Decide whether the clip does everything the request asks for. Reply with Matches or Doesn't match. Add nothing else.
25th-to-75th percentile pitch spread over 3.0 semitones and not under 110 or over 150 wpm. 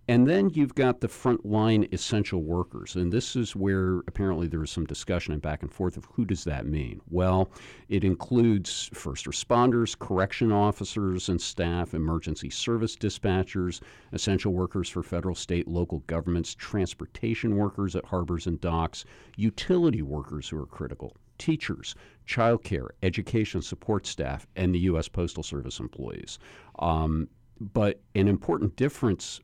Matches